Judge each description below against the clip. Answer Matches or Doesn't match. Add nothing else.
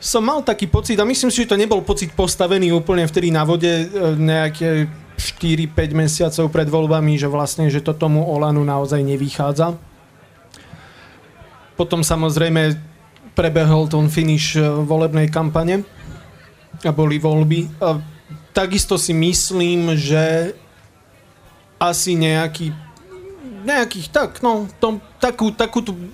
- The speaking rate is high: Doesn't match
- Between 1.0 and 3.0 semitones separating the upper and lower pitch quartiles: Doesn't match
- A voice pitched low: Doesn't match